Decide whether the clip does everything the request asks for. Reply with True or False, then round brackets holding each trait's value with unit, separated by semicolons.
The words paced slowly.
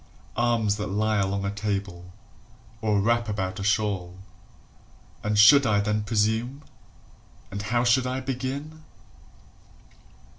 True (120 wpm)